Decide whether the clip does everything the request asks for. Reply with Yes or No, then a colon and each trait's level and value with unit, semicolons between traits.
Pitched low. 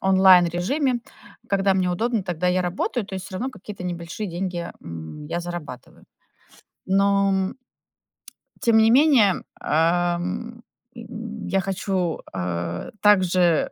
No: medium, 185 Hz